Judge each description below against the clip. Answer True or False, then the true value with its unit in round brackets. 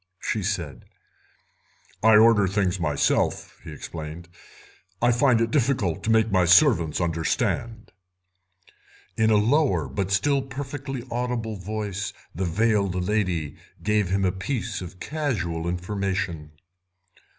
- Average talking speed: False (125 wpm)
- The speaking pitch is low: True (100 Hz)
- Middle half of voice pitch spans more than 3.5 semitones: True (4.6 semitones)